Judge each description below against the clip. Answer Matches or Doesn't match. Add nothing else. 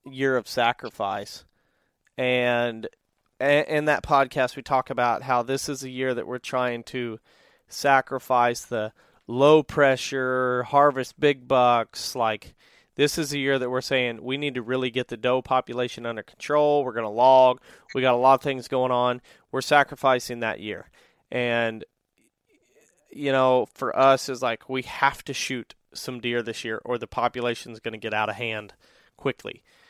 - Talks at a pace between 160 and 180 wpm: Matches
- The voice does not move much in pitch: Matches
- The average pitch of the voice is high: Doesn't match